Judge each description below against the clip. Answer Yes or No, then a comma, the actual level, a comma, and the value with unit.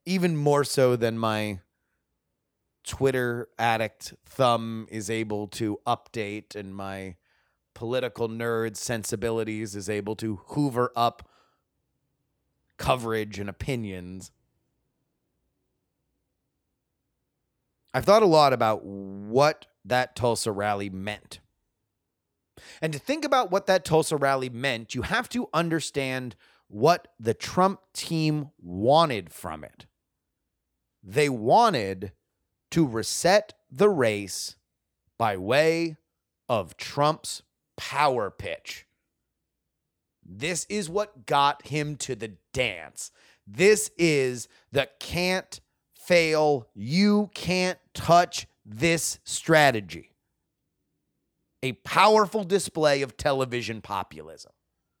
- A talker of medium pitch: No, low, 125 Hz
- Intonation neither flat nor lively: No, wide, 6.7 semitones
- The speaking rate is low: Yes, slow, 100 wpm